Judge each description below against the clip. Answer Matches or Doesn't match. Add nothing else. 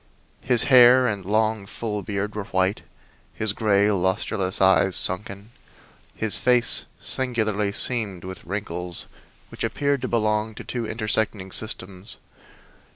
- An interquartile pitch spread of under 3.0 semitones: Matches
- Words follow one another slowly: Matches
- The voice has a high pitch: Doesn't match